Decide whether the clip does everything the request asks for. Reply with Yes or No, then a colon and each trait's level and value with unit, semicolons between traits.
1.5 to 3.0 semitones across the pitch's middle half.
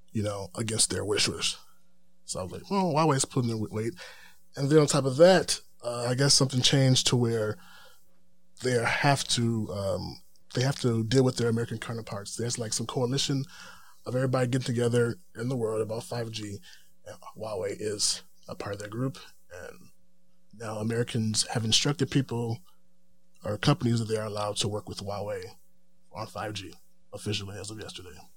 No: average, 4.3 semitones